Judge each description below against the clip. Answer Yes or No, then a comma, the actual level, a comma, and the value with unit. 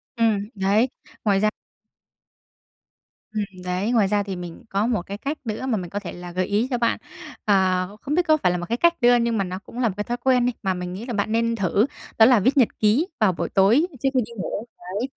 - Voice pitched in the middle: No, high, 215 Hz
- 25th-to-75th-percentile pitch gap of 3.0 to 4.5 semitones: Yes, average, 4.0 semitones